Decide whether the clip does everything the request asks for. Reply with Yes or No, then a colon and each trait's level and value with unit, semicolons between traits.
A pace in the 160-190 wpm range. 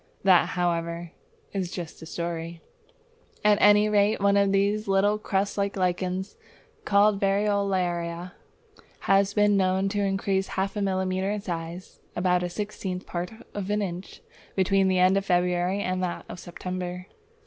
No: average, 150 wpm